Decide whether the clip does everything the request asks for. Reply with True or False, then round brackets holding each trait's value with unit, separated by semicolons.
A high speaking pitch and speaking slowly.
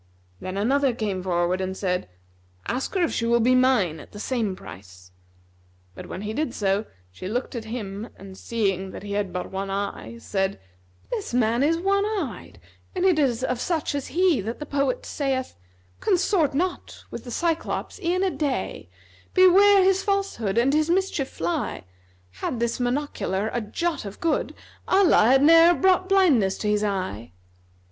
False (240 Hz; 180 wpm)